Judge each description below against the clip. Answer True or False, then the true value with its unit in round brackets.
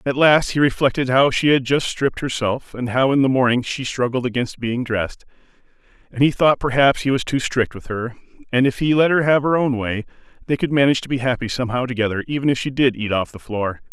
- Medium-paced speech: False (235 wpm)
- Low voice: True (130 Hz)